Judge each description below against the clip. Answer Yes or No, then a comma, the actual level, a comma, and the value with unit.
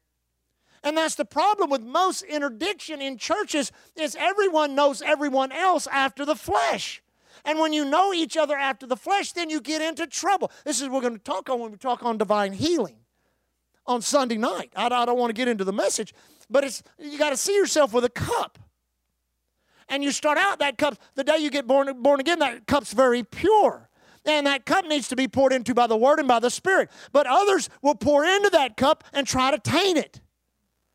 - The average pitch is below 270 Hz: No, very high, 285 Hz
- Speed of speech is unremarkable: No, fast, 215 wpm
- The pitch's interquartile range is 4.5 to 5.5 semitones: No, average, 3.9 semitones